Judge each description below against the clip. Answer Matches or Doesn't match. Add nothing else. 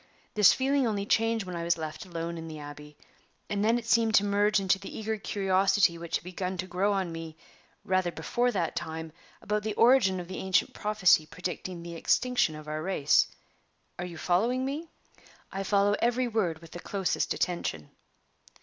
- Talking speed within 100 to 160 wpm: Doesn't match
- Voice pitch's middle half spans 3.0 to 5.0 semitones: Matches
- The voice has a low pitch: Doesn't match